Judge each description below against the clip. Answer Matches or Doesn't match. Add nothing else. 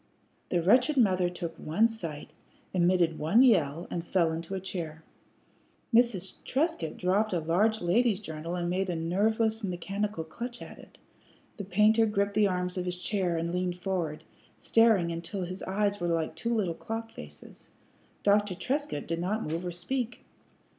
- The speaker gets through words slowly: Doesn't match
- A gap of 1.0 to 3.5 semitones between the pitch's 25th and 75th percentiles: Doesn't match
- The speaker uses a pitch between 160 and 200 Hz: Matches